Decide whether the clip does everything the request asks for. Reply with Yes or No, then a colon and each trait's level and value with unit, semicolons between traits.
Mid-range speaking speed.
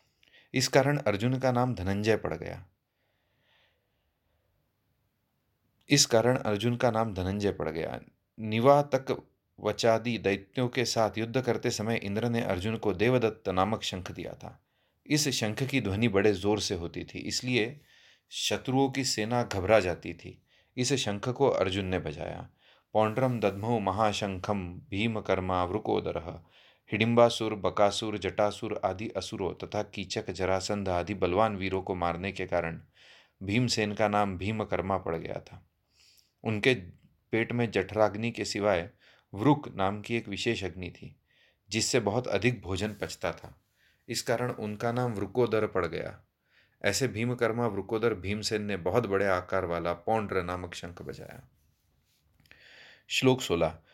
Yes: average, 135 wpm